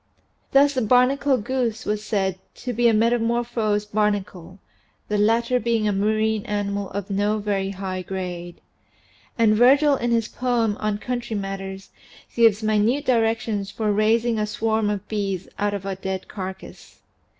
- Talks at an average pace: Yes, average, 155 wpm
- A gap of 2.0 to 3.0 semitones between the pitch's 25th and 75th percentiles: Yes, average, 2.7 semitones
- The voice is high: Yes, high, 215 Hz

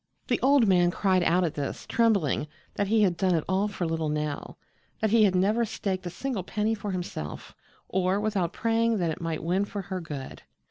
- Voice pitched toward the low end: No, high, 190 Hz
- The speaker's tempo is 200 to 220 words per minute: Yes, fast, 205 wpm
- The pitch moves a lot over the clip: No, average, 3.8 semitones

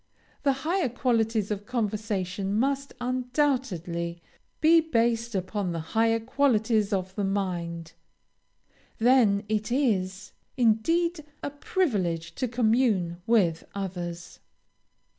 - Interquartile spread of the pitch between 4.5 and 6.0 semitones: Yes, average, 5.2 semitones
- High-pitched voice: Yes, high, 220 Hz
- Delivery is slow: Yes, slow, 105 wpm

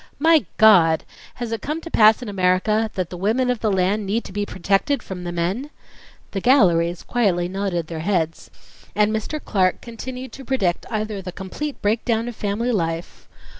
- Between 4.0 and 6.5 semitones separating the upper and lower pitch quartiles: Yes, average, 4.6 semitones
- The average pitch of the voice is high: Yes, high, 205 Hz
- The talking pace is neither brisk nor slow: Yes, average, 180 wpm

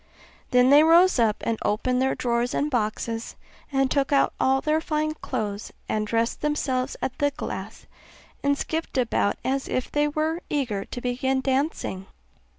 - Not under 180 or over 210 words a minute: No, average, 160 wpm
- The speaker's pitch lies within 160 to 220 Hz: No, very high, 265 Hz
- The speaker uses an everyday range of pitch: Yes, average, 3.8 semitones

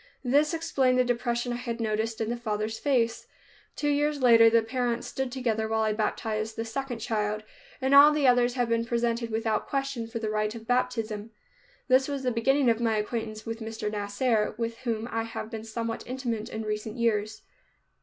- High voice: Yes, high, 230 Hz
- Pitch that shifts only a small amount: Yes, narrow, 2.3 semitones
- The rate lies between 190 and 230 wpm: Yes, average, 195 wpm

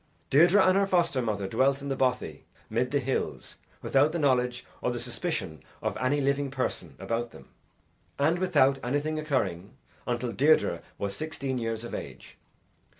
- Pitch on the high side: No, low, 135 Hz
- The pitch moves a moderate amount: Yes, average, 3.8 semitones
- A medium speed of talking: Yes, average, 160 wpm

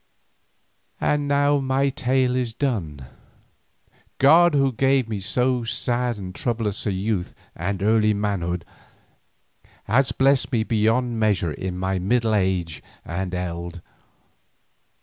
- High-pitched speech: No, low, 110 Hz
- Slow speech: Yes, slow, 120 wpm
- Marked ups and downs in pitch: Yes, wide, 5.7 semitones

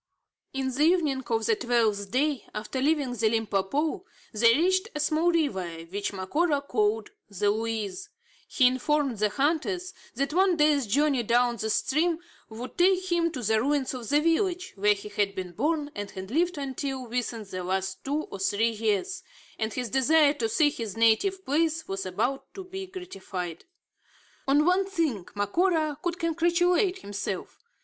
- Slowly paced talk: No, average, 165 wpm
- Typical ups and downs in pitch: No, wide, 7.5 semitones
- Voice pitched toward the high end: Yes, very high, 270 Hz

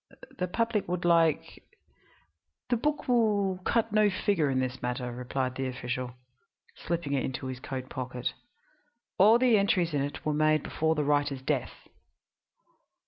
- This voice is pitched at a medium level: Yes, medium, 150 Hz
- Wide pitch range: Yes, wide, 7.2 semitones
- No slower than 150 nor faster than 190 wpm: Yes, average, 155 wpm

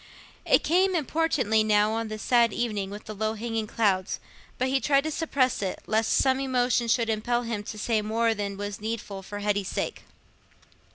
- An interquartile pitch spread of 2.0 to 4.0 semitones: Yes, average, 3.2 semitones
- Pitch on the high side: Yes, high, 225 Hz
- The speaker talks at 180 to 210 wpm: Yes, average, 185 wpm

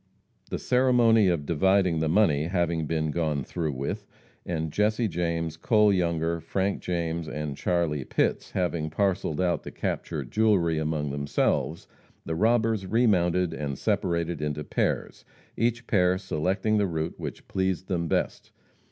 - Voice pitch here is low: Yes, very low, 85 Hz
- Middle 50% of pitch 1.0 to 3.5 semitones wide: No, average, 3.9 semitones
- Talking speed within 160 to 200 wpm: No, average, 145 wpm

